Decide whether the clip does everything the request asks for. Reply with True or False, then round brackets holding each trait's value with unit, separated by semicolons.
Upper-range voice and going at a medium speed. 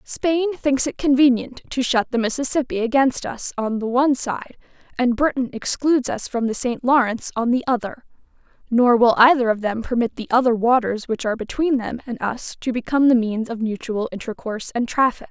True (245 Hz; 190 wpm)